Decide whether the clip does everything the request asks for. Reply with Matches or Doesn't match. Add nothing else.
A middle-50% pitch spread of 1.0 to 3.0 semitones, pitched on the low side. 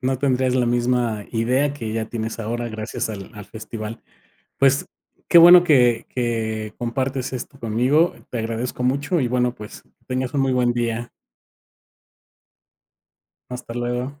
Matches